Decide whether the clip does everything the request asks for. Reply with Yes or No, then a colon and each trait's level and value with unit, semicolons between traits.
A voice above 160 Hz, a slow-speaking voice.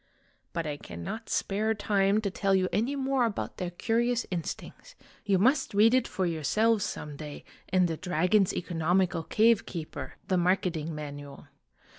No: high, 190 Hz; average, 160 wpm